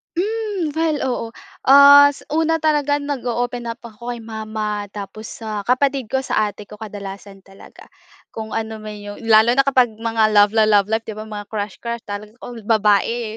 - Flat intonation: No, average, 4.0 semitones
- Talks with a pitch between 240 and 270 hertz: No, high, 225 Hz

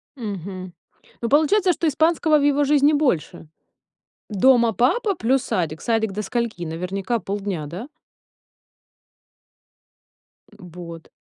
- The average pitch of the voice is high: Yes, high, 225 Hz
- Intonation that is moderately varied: No, wide, 7.8 semitones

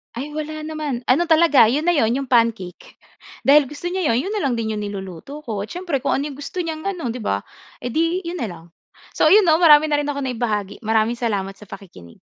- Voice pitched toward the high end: Yes, very high, 275 Hz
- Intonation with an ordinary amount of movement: No, wide, 6.1 semitones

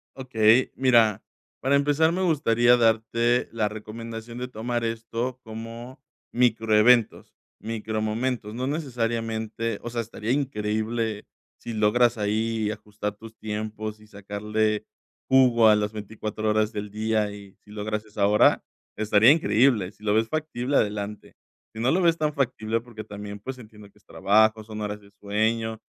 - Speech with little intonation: Yes, narrow, 2.1 semitones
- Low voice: Yes, low, 110 Hz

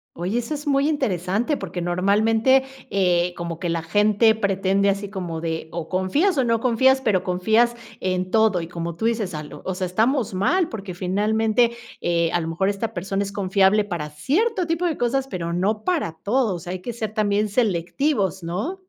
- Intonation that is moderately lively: Yes, average, 4.7 semitones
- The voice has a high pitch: Yes, high, 200 Hz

